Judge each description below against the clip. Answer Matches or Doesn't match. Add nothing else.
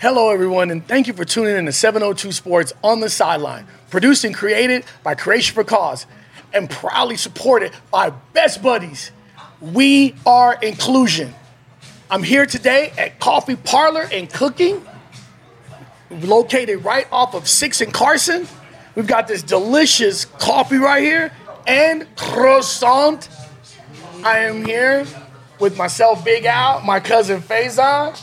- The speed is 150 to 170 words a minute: Doesn't match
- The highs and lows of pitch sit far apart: Matches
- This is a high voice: Matches